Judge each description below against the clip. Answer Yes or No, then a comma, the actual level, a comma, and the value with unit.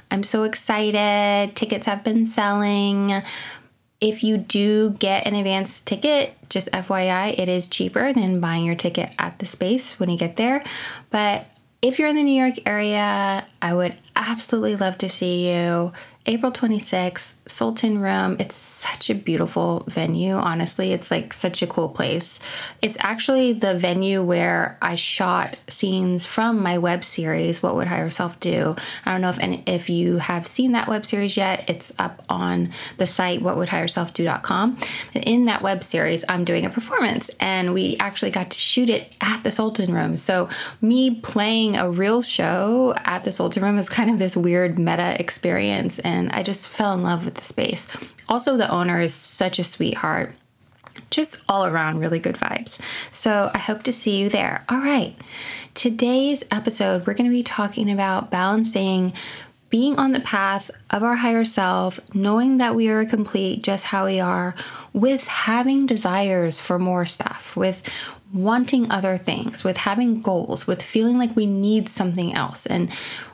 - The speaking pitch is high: Yes, high, 200 Hz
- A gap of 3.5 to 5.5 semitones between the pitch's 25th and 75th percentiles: Yes, average, 4.1 semitones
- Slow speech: No, average, 175 wpm